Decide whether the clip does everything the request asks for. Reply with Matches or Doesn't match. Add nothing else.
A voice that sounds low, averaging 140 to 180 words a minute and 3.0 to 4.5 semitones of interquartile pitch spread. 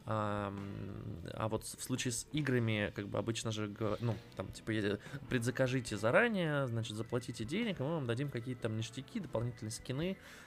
Matches